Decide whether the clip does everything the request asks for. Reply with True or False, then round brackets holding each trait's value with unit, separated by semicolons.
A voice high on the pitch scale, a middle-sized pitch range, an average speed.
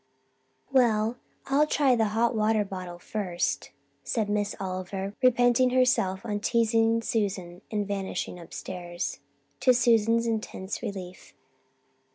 False (215 Hz; 3.7 semitones; 115 wpm)